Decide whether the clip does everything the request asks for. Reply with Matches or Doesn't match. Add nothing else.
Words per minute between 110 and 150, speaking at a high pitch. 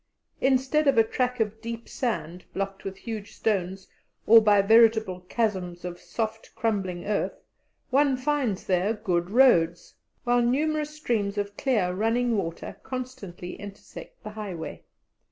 Matches